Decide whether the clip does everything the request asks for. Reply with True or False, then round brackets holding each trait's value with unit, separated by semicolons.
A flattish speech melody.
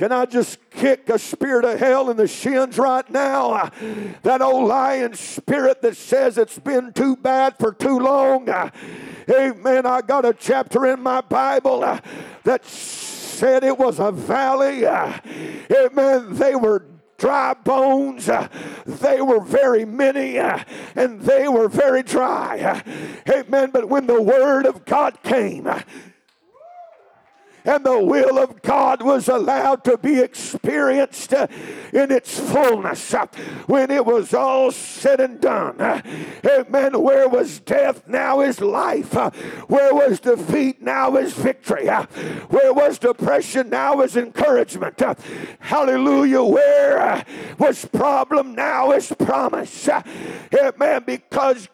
True (1.6 semitones)